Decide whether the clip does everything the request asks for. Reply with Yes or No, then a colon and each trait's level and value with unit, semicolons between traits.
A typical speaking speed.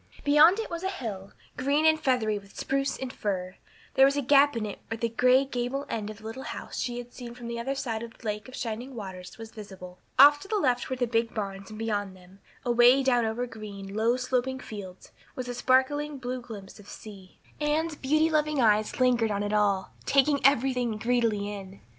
No: fast, 215 wpm